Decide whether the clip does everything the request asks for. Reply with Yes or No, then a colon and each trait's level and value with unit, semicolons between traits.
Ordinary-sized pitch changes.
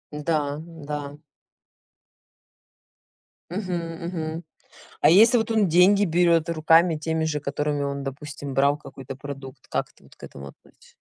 Yes: average, 3.1 semitones